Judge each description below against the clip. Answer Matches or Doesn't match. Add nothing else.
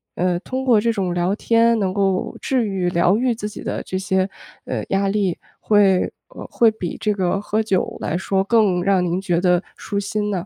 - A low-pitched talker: Doesn't match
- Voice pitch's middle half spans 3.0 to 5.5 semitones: Doesn't match